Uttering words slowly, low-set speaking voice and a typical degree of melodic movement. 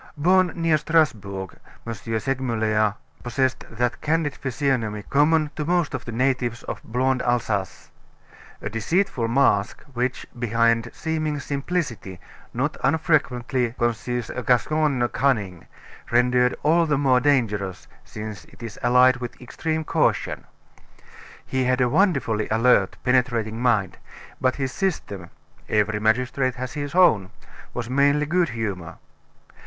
Yes: slow, 125 wpm; low, 125 Hz; average, 4.2 semitones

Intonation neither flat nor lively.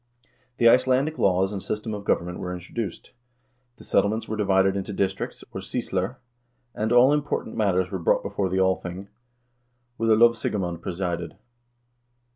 Yes: average, 3.3 semitones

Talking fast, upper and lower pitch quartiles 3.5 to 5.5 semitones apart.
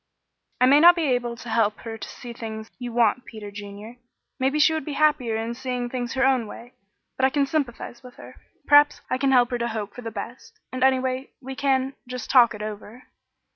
No: fast, 220 wpm; average, 2.7 semitones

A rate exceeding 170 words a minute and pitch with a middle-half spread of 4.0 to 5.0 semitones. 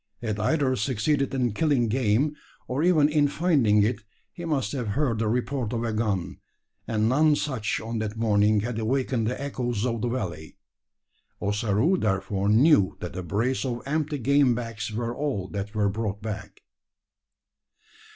No: average, 160 wpm; average, 4.5 semitones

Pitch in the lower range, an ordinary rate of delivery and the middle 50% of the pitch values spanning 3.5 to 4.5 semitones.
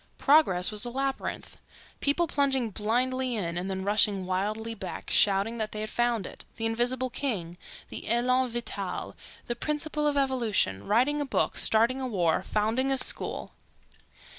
No: high, 235 Hz; average, 150 wpm; average, 4.0 semitones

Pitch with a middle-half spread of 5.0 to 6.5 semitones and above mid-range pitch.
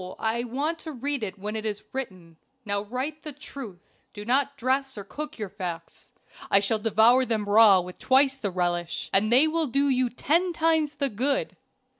Yes: wide, 5.5 semitones; high, 240 Hz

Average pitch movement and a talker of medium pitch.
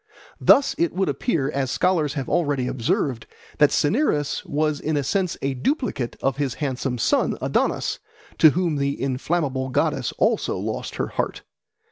Yes: average, 3.9 semitones; medium, 145 Hz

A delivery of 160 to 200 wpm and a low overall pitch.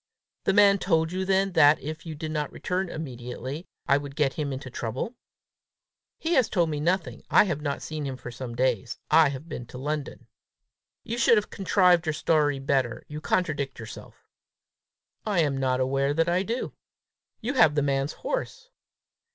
No: average, 180 wpm; medium, 155 Hz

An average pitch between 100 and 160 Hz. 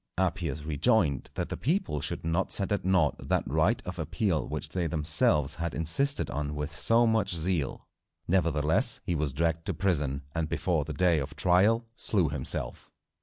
No: very low, 80 Hz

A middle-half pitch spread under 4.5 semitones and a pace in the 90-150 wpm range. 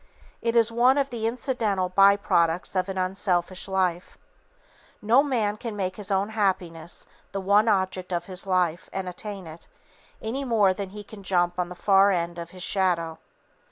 No: average, 2.9 semitones; average, 180 wpm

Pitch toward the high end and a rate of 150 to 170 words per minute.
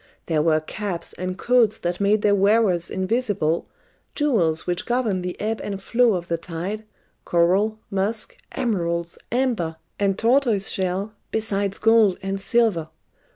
No: high, 195 Hz; slow, 135 wpm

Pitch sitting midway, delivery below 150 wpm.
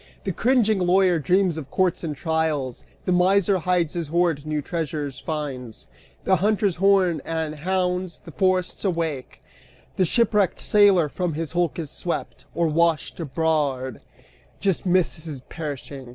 Yes: medium, 170 Hz; average, 140 wpm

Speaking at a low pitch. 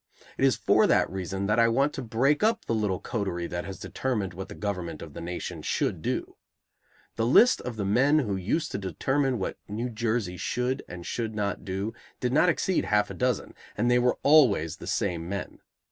Yes: low, 110 Hz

